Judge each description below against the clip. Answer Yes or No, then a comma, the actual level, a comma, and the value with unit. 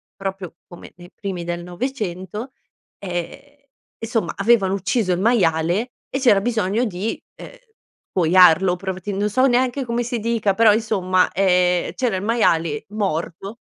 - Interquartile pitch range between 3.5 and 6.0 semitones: Yes, average, 4.3 semitones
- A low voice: No, high, 195 Hz